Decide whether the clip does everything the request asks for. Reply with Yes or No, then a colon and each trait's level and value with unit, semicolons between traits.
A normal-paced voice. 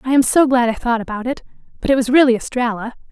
No: fast, 250 wpm